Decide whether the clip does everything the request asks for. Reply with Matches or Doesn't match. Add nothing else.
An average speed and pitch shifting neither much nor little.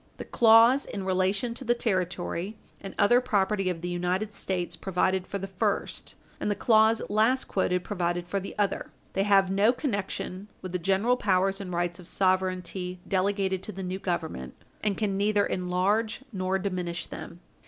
Doesn't match